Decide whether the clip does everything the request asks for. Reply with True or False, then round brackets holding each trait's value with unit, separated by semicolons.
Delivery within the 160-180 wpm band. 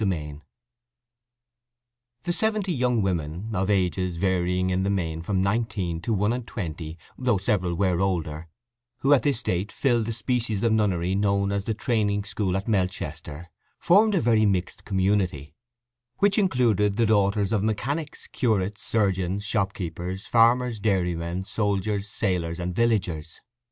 False (145 wpm)